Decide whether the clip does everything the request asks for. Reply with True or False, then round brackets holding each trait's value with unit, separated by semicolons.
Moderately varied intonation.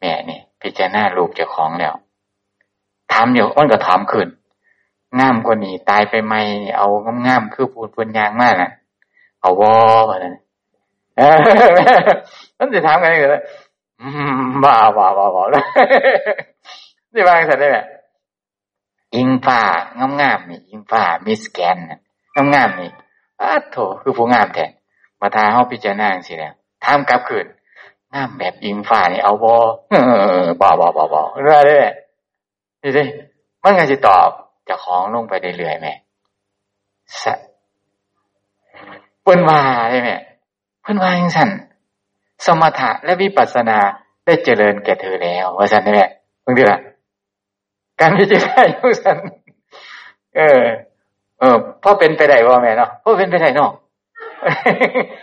False (6.4 semitones)